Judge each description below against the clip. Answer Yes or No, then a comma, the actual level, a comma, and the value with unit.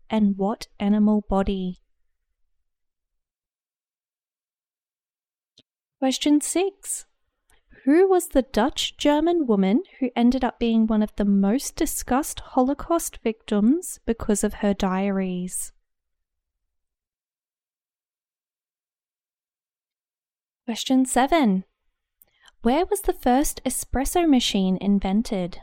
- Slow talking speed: Yes, slow, 85 wpm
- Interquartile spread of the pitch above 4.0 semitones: Yes, wide, 5.6 semitones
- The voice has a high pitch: Yes, high, 225 Hz